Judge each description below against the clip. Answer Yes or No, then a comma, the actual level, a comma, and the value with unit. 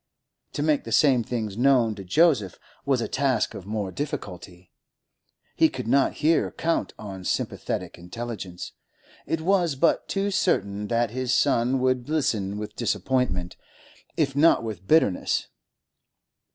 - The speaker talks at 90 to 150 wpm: Yes, average, 140 wpm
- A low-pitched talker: Yes, low, 120 Hz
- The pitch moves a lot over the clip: Yes, wide, 5.7 semitones